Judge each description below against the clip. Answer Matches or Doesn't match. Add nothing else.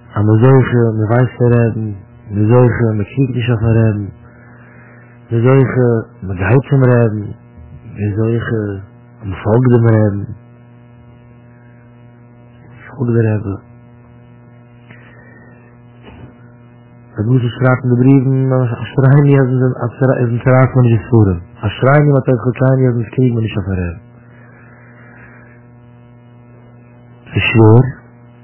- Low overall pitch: Matches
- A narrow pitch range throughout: Matches